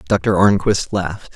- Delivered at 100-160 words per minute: Yes, slow, 135 wpm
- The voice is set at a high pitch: No, very low, 95 Hz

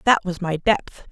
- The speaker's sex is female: Yes, female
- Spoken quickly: Yes, fast, 215 wpm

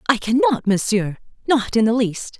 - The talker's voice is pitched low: No, high, 225 Hz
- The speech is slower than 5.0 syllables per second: Yes, 4.8 syllables/s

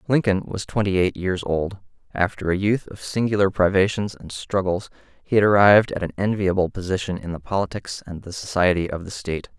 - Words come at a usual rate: Yes, average, 190 wpm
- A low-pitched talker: Yes, very low, 95 Hz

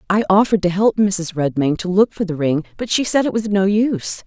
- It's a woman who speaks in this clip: Yes, female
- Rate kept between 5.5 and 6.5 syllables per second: Yes, 5.7 syllables/s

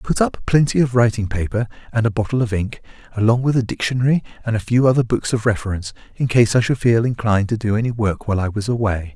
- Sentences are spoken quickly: Yes, fast, 240 wpm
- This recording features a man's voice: Yes, male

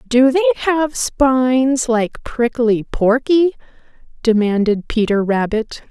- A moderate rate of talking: No, slow, 100 wpm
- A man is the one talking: No, female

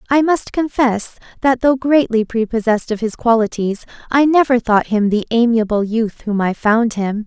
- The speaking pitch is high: Yes, high, 230 Hz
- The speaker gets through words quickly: No, average, 175 wpm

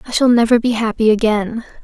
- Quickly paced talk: No, average, 195 wpm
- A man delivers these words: No, female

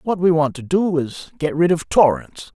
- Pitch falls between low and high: Yes, medium, 160 Hz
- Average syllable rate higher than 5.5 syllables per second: No, 5.0 syllables/s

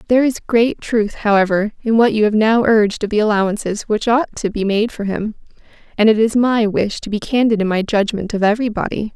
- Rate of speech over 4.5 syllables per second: Yes, 5.7 syllables/s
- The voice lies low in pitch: No, high, 215 Hz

